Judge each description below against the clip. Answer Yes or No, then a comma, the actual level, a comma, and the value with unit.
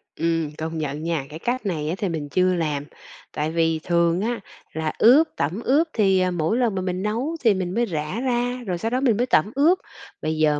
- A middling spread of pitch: No, wide, 6.8 semitones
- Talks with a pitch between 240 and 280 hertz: No, medium, 185 Hz